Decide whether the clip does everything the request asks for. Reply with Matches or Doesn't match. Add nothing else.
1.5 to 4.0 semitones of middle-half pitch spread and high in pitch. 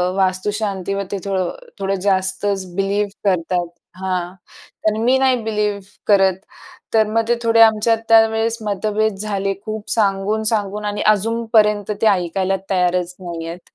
Matches